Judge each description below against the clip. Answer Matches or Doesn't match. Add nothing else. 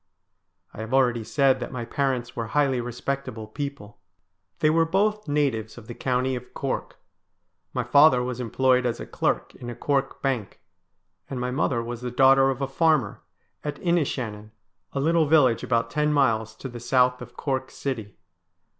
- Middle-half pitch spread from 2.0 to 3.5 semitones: Matches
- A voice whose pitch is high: Doesn't match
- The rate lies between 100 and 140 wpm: Doesn't match